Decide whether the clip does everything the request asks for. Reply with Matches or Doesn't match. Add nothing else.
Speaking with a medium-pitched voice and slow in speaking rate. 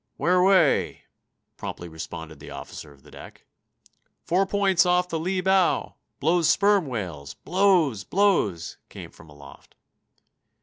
Matches